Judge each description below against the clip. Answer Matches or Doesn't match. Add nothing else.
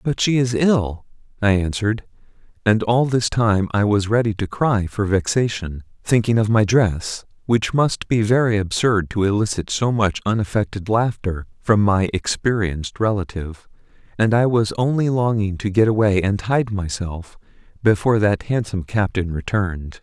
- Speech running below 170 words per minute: Matches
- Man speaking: Matches